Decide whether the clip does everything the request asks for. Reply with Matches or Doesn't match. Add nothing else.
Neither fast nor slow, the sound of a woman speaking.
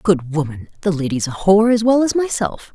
Matches